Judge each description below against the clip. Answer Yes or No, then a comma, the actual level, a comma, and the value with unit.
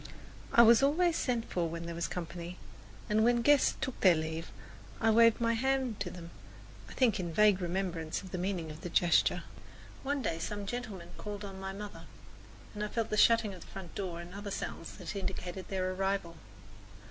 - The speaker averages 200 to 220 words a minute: Yes, fast, 205 wpm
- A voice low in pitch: No, high, 195 Hz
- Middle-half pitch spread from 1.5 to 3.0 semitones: No, average, 4.5 semitones